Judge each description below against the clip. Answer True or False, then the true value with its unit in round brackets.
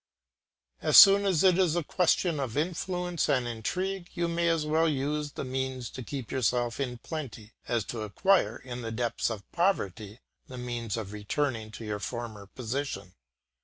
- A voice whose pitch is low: True (130 Hz)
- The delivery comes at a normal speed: True (170 wpm)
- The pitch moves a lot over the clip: True (6.4 semitones)